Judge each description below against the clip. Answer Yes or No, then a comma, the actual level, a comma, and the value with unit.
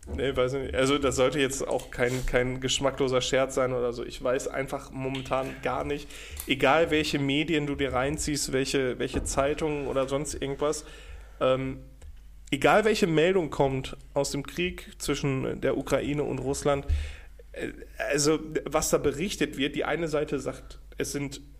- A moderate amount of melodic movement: No, narrow, 2.1 semitones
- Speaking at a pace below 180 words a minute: Yes, average, 160 wpm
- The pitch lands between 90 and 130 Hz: No, medium, 140 Hz